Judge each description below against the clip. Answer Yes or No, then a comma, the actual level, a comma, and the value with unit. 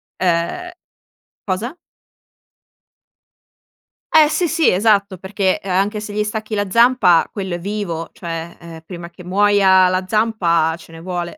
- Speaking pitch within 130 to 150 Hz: No, high, 190 Hz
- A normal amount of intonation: Yes, average, 3.5 semitones